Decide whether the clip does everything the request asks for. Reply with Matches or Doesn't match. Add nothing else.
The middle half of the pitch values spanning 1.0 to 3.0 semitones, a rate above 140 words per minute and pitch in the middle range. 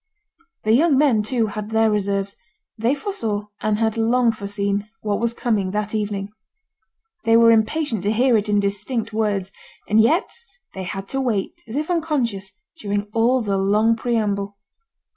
Doesn't match